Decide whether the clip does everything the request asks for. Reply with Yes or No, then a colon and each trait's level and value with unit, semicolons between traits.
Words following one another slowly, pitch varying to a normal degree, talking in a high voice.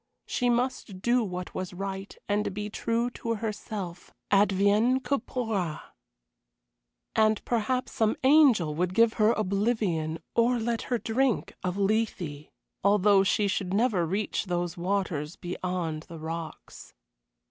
Yes: slow, 130 wpm; average, 4.1 semitones; high, 205 Hz